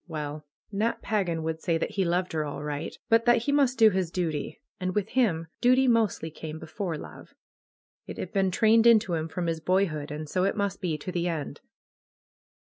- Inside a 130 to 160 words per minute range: No, fast, 205 wpm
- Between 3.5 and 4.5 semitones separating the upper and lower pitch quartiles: No, average, 5.0 semitones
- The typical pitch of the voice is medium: Yes, medium, 180 Hz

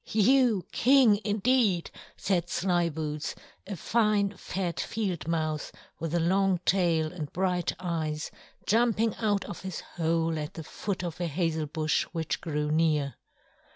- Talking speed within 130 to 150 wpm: Yes, average, 140 wpm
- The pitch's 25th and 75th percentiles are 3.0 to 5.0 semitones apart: Yes, average, 4.0 semitones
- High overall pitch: No, medium, 175 Hz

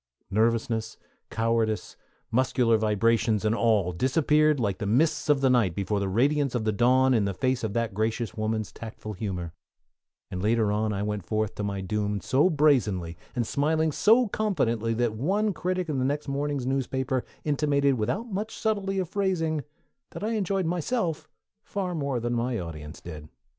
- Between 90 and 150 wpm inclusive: No, average, 170 wpm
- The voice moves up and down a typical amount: No, wide, 5.9 semitones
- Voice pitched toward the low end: Yes, low, 120 Hz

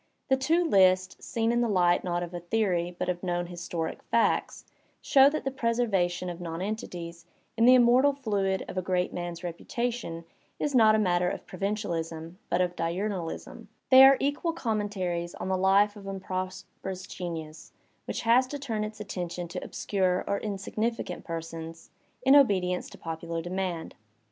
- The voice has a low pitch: No, medium, 185 Hz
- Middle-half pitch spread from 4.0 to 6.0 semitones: Yes, average, 4.3 semitones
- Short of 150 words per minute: No, average, 165 wpm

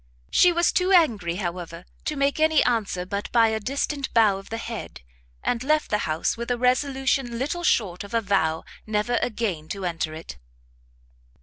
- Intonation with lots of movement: Yes, wide, 5.9 semitones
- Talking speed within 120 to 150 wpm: No, average, 180 wpm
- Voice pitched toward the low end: No, high, 225 Hz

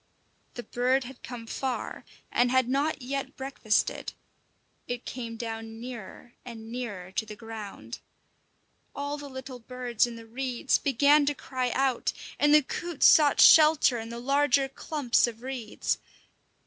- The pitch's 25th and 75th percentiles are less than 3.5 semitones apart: Yes, average, 2.9 semitones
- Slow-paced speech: No, average, 150 wpm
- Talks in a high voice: Yes, very high, 250 Hz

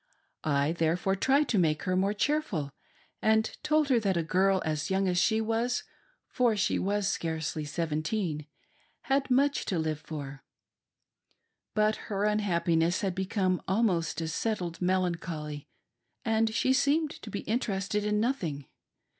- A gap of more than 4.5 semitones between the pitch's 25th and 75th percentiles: Yes, average, 5.1 semitones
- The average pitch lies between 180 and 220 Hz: Yes, high, 190 Hz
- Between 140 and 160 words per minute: Yes, average, 150 wpm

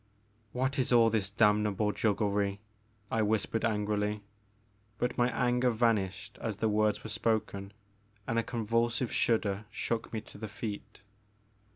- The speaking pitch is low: Yes, low, 110 Hz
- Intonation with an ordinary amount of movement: No, narrow, 2.0 semitones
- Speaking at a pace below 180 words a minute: Yes, average, 140 wpm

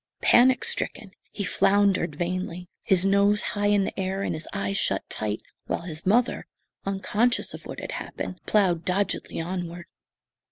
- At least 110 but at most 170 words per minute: Yes, average, 155 wpm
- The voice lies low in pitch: No, high, 190 Hz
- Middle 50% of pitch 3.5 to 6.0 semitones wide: No, average, 2.8 semitones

